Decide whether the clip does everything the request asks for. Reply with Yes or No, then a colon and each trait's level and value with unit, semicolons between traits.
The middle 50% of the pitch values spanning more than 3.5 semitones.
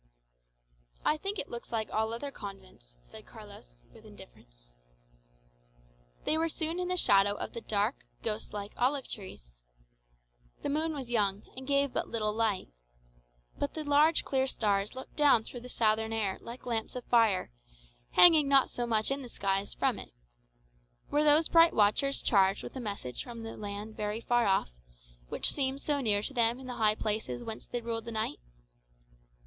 Yes: average, 5.0 semitones